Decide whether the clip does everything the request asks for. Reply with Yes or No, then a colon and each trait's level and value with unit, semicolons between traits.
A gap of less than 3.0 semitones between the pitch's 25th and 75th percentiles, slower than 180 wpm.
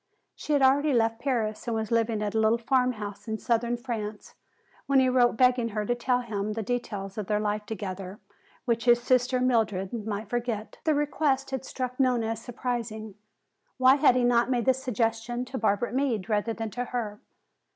No: narrow, 2.6 semitones; average, 190 wpm